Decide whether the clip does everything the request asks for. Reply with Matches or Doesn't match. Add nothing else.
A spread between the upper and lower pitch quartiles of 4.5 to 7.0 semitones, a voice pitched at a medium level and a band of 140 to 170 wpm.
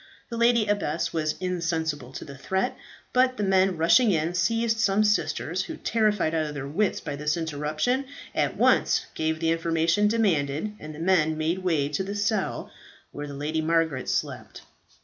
Doesn't match